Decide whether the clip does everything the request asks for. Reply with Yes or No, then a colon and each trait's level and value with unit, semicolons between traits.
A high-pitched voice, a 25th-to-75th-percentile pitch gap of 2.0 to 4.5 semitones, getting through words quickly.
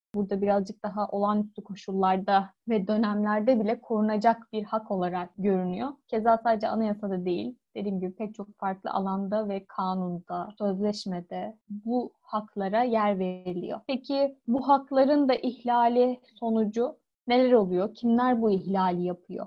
No: high, 210 Hz; average, 3.2 semitones; average, 130 wpm